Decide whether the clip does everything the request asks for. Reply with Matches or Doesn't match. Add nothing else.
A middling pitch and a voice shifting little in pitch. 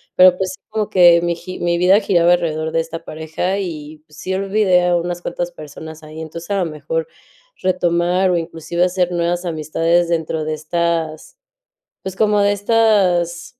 Matches